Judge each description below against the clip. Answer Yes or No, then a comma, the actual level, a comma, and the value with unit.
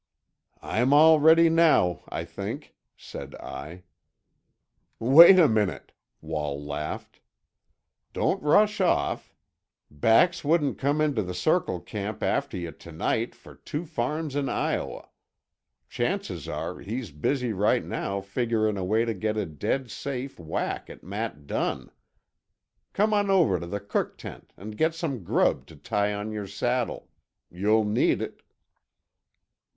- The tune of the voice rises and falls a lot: Yes, wide, 7.8 semitones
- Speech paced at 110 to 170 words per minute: Yes, average, 140 wpm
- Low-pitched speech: Yes, low, 110 Hz